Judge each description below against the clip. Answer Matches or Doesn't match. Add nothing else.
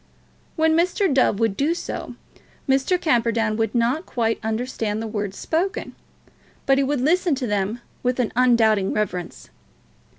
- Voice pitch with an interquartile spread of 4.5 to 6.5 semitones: Matches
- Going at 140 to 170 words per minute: Matches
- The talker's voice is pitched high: Matches